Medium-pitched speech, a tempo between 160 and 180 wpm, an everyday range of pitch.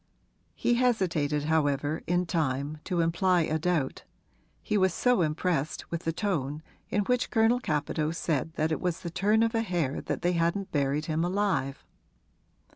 Yes: medium, 165 Hz; average, 165 wpm; average, 4.0 semitones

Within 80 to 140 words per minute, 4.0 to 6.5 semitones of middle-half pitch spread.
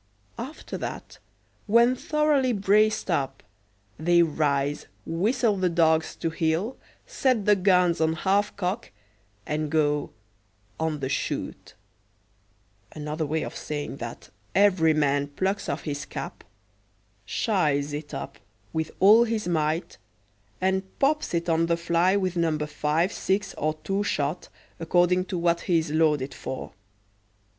Yes: slow, 135 wpm; average, 4.3 semitones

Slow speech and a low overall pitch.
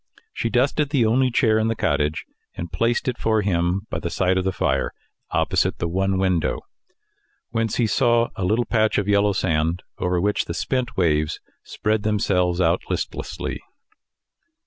No: average, 170 wpm; low, 100 Hz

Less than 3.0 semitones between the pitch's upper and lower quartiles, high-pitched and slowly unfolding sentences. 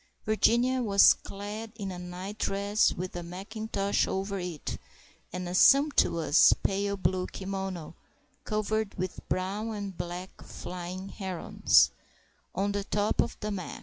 Yes: narrow, 2.4 semitones; high, 195 Hz; slow, 130 wpm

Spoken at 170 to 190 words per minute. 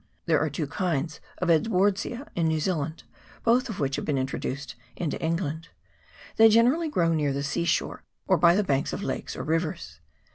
Yes: average, 185 wpm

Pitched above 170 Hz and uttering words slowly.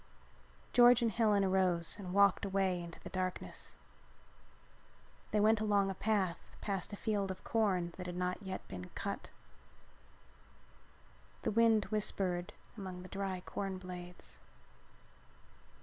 Yes: high, 190 Hz; slow, 130 wpm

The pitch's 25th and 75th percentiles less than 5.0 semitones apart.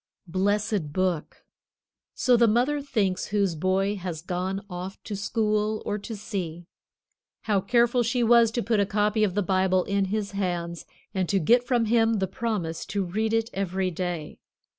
Yes: average, 3.2 semitones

